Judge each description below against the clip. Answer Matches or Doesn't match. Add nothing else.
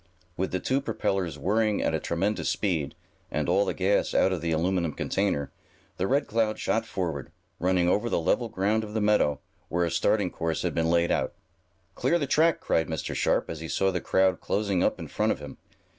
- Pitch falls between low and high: Doesn't match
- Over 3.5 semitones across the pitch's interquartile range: Matches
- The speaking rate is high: Matches